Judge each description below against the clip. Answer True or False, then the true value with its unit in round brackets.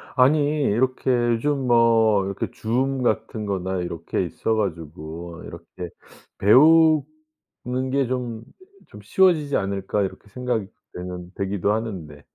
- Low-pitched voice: True (110 Hz)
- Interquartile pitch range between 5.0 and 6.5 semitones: True (5.4 semitones)